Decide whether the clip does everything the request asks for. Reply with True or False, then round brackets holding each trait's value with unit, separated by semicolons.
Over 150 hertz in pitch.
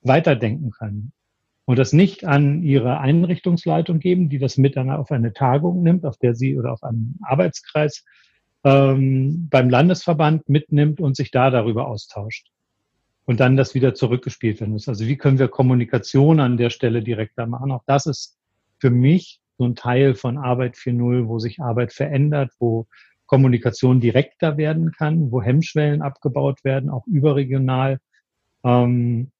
False (135 Hz)